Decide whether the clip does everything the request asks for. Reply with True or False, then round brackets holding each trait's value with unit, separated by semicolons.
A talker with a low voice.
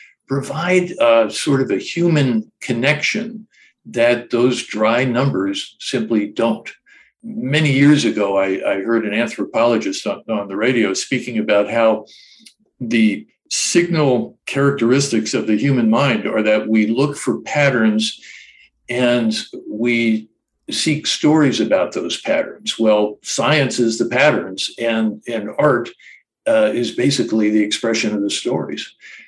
True (125 Hz)